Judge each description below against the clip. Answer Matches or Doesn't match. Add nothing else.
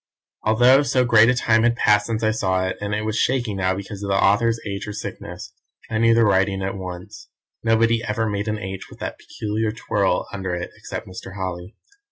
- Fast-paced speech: Matches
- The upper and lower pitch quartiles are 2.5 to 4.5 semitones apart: Matches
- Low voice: Matches